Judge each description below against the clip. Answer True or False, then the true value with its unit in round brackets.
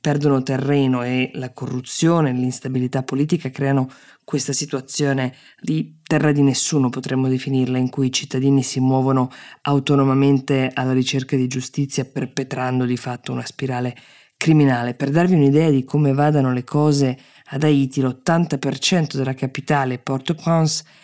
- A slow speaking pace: False (135 wpm)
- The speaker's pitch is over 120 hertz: True (135 Hz)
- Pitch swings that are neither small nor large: False (1.9 semitones)